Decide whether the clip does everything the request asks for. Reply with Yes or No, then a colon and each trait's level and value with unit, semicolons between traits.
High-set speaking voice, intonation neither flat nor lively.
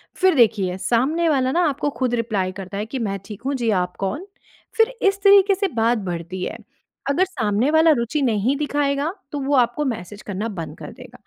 No: high, 245 Hz; wide, 6.5 semitones